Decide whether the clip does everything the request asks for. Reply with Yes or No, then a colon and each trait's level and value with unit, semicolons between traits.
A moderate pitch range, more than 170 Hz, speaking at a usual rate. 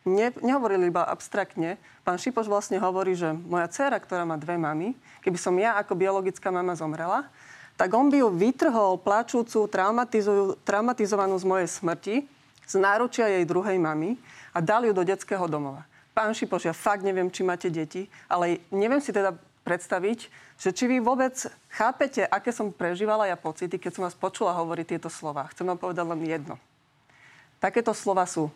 No: average, 3.7 semitones; high, 190 Hz; fast, 170 wpm